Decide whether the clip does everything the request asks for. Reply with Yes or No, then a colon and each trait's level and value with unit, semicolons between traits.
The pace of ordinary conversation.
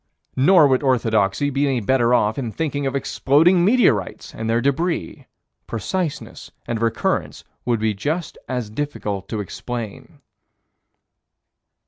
No: slow, 125 wpm